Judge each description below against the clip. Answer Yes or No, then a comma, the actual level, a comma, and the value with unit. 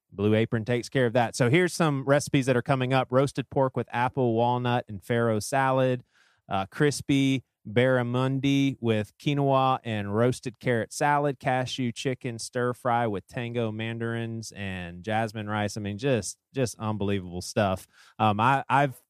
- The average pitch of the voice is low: Yes, low, 120 Hz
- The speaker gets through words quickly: No, average, 155 wpm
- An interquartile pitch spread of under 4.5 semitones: Yes, average, 3.4 semitones